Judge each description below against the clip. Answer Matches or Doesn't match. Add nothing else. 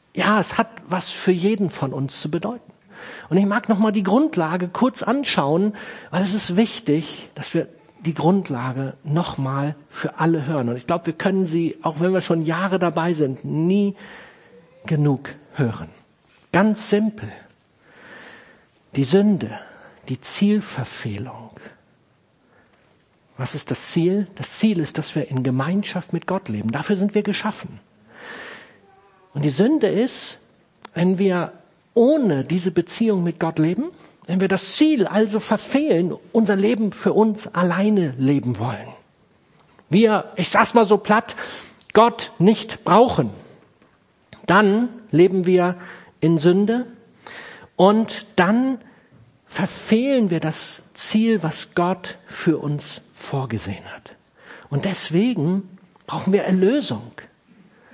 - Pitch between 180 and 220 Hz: Matches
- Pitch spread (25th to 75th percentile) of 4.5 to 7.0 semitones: Matches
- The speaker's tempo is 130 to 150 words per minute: Matches